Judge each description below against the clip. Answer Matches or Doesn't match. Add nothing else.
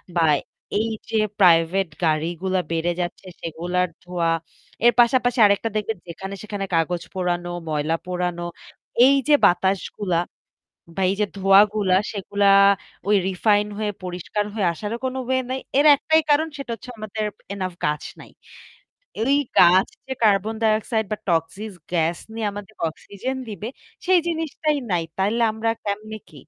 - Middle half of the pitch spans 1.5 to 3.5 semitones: Doesn't match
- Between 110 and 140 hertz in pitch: Doesn't match